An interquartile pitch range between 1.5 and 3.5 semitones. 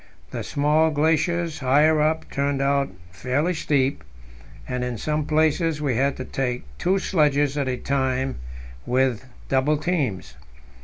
Yes: average, 2.8 semitones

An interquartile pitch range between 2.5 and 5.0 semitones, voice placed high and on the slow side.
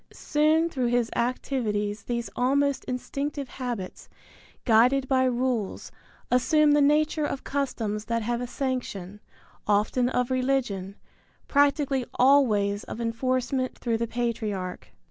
Yes: average, 3.4 semitones; very high, 250 Hz; slow, 120 wpm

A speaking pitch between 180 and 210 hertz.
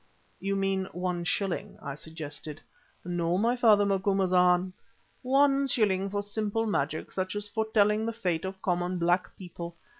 Yes: high, 190 Hz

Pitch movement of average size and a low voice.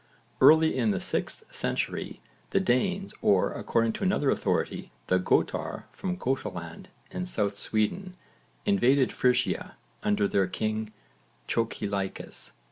No: wide, 7.7 semitones; low, 115 Hz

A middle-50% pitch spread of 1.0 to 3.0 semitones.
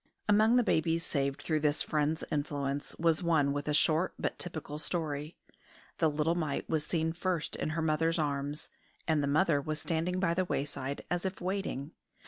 Yes: narrow, 2.6 semitones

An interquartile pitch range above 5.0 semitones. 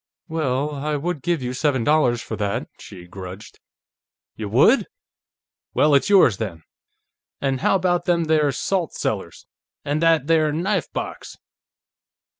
Yes: wide, 5.6 semitones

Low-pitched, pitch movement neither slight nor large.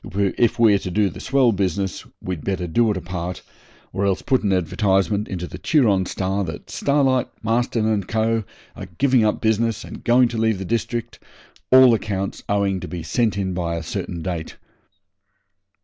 Yes: low, 100 Hz; average, 3.7 semitones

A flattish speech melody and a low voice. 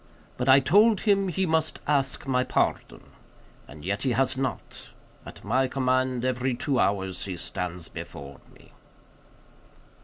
No: wide, 5.6 semitones; low, 130 Hz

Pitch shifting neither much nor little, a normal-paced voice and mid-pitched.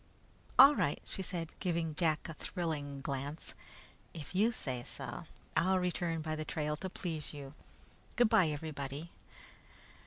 Yes: average, 3.6 semitones; average, 145 wpm; medium, 160 Hz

